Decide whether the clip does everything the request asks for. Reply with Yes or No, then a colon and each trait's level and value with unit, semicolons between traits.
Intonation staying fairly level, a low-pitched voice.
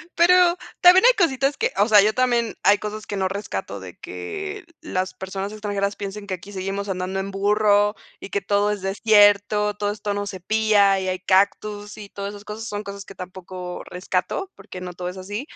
No: narrow, 1.8 semitones; high, 205 Hz